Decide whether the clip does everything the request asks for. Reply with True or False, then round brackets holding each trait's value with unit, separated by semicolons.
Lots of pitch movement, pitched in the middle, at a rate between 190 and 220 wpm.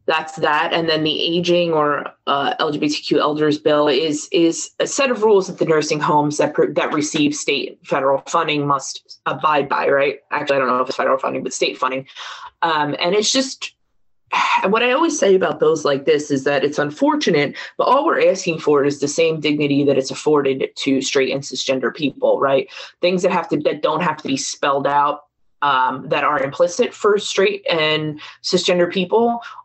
True (8.3 semitones; 160 Hz; 200 wpm)